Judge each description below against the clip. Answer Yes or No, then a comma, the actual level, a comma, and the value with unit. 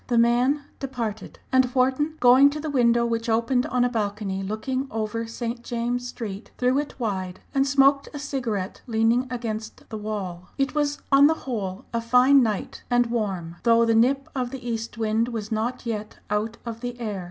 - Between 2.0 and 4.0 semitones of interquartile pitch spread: Yes, average, 3.0 semitones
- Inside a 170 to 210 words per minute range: Yes, average, 185 wpm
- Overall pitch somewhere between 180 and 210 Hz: No, high, 235 Hz